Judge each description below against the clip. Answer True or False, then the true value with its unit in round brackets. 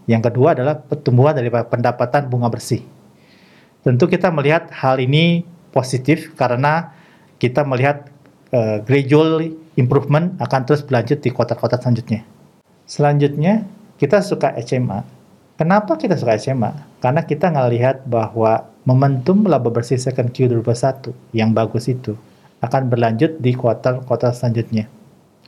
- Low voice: True (130 Hz)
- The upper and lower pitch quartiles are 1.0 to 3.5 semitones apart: False (4.1 semitones)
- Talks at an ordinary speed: True (120 wpm)